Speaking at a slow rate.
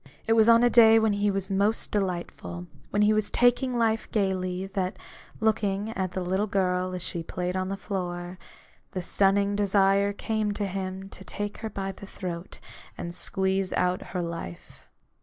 No: average, 175 wpm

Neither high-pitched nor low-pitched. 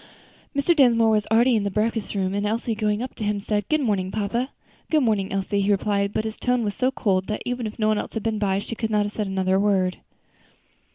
No: high, 210 Hz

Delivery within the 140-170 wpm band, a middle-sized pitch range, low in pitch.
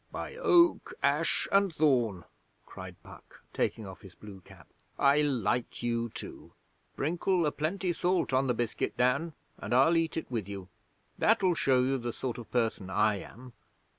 No: average, 165 wpm; wide, 6.5 semitones; low, 130 Hz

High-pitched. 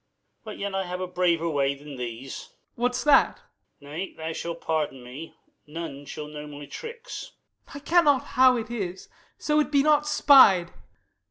No: medium, 180 Hz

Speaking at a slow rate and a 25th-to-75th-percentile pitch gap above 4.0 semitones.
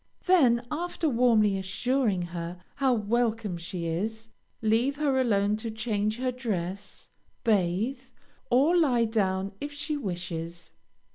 Yes: slow, 125 wpm; average, 5.1 semitones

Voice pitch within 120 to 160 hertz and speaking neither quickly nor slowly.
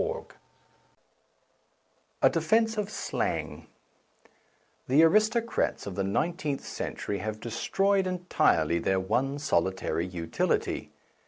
No: low, 135 Hz; slow, 95 wpm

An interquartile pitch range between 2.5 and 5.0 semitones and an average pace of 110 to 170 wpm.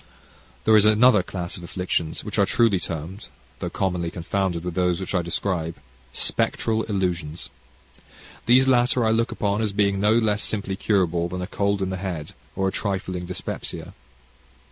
Yes: average, 3.0 semitones; average, 165 wpm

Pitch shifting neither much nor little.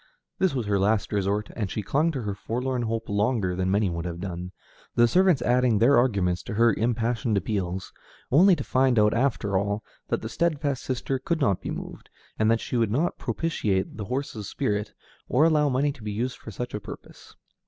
Yes: average, 4.4 semitones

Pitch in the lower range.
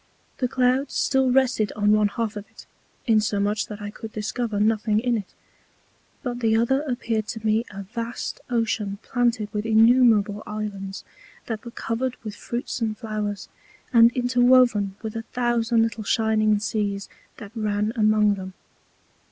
No: high, 220 Hz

